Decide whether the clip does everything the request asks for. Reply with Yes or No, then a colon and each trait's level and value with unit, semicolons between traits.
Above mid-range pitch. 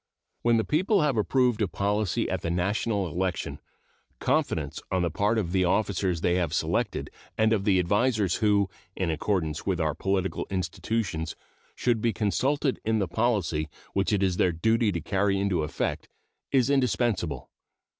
No: low, 100 Hz